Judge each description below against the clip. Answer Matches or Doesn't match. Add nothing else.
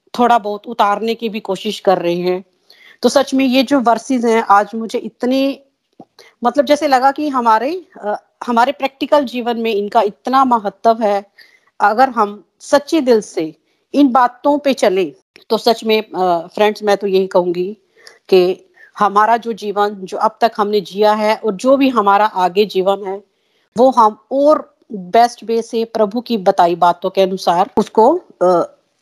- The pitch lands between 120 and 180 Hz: Doesn't match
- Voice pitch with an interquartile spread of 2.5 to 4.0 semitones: Doesn't match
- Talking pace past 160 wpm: Matches